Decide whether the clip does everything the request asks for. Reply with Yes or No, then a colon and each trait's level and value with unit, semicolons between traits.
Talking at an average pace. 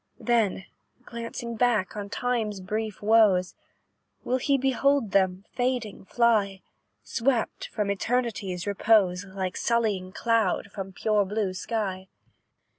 No: slow, 115 wpm